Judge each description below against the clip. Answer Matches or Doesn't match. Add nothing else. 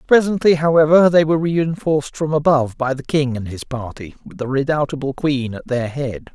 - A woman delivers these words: Doesn't match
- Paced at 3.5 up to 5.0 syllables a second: Doesn't match